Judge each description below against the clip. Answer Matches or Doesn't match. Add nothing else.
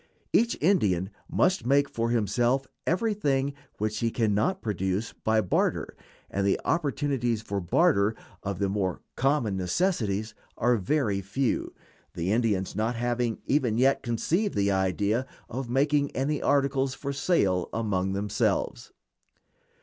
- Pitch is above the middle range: Doesn't match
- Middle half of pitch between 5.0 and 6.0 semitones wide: Matches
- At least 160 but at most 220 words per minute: Doesn't match